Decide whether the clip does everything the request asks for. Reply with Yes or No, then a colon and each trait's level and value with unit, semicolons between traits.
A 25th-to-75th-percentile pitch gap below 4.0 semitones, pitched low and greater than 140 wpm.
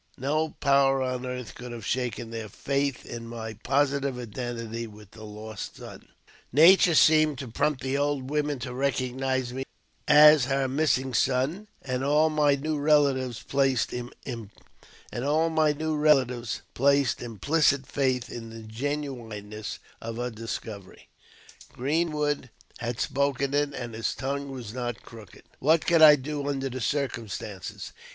No: average, 3.4 semitones; low, 130 Hz; slow, 135 wpm